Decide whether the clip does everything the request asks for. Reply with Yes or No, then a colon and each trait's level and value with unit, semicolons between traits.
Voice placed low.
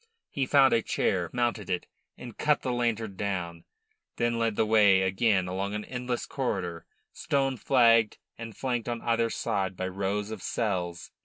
Yes: low, 110 Hz